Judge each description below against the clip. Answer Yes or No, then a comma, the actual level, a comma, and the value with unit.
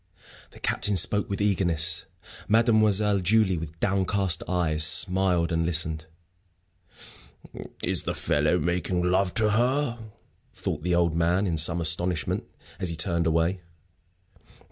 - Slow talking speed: Yes, slow, 125 wpm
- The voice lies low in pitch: Yes, very low, 90 Hz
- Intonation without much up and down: No, average, 3.3 semitones